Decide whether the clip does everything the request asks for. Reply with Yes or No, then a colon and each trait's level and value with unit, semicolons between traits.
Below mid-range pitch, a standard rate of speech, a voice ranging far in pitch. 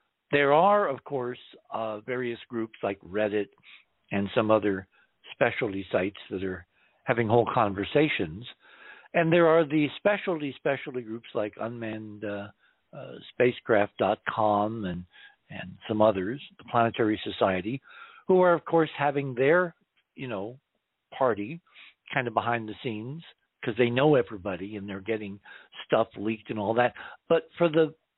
Yes: low, 120 Hz; average, 145 wpm; wide, 5.8 semitones